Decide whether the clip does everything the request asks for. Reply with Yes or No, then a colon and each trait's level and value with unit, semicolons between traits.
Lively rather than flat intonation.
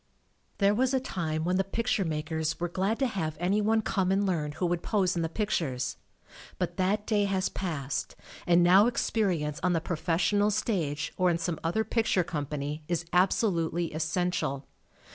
No: average, 4.0 semitones